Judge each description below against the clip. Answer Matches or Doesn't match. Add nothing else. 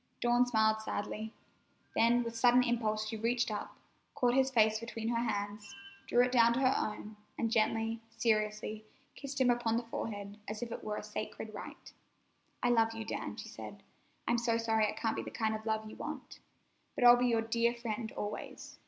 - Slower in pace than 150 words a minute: Doesn't match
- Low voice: Doesn't match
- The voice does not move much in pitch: Matches